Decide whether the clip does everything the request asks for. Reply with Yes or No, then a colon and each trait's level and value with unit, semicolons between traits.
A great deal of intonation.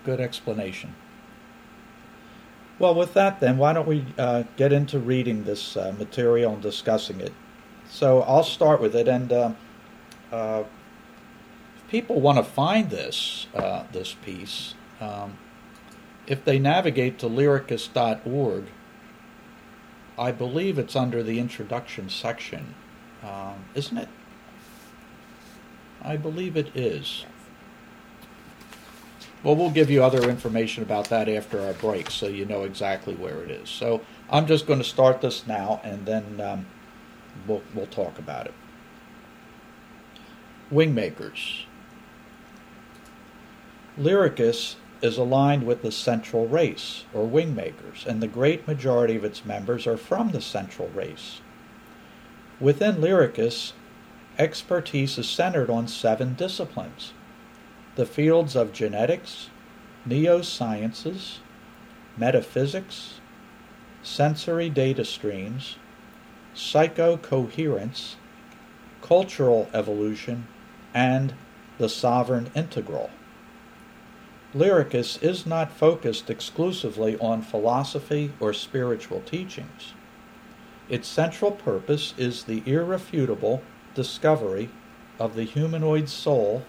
Yes: wide, 6.2 semitones